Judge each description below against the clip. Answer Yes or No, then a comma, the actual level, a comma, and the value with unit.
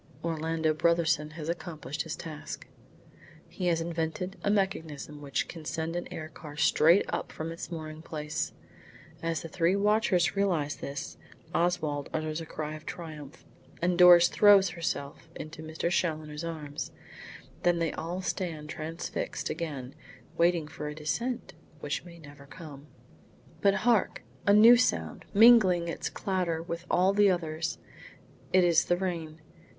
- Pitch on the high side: No, medium, 165 Hz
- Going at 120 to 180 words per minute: Yes, average, 145 wpm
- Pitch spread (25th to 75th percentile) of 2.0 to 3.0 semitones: Yes, narrow, 2.4 semitones